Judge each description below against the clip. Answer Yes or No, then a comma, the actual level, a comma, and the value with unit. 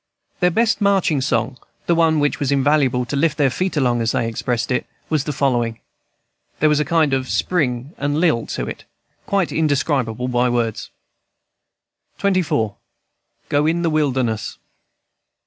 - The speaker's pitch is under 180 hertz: Yes, medium, 140 Hz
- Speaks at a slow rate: No, average, 155 wpm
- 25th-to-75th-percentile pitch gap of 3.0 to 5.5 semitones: Yes, average, 4.4 semitones